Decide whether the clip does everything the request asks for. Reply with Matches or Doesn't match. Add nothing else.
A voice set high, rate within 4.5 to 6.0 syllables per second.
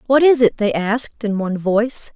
Matches